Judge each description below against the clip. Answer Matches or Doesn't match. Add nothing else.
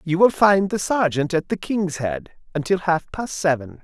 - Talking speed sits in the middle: Matches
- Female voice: Doesn't match